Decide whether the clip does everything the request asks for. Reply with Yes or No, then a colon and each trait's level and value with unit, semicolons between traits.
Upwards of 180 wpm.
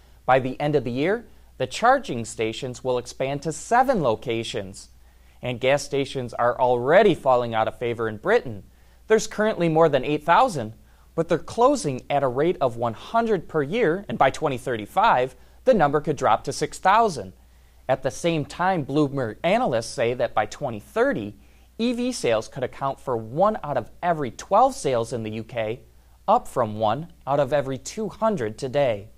No: average, 165 wpm